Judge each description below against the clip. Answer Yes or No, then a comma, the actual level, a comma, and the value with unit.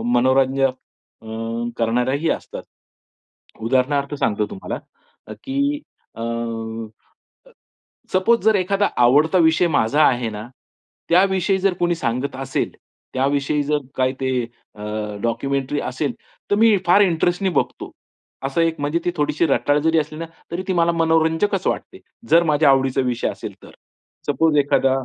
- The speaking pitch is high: No, medium, 145 Hz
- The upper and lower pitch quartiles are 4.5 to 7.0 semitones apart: Yes, average, 4.8 semitones